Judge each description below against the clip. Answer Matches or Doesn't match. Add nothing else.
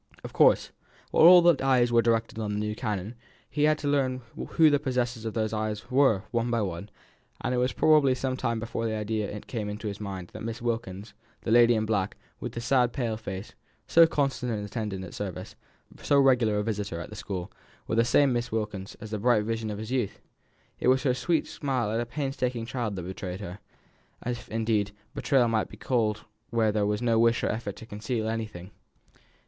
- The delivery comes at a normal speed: Doesn't match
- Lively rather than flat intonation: Doesn't match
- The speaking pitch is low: Matches